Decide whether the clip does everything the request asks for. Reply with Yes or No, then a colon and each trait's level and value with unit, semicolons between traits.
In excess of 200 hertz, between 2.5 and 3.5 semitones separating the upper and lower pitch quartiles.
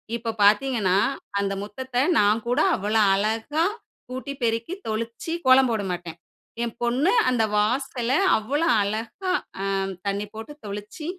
No: high, 230 Hz; average, 3.9 semitones